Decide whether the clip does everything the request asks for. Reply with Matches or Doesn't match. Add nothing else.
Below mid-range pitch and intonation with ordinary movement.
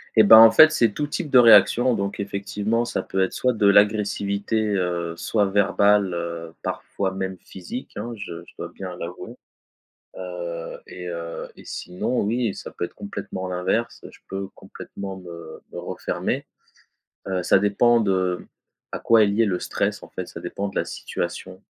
Matches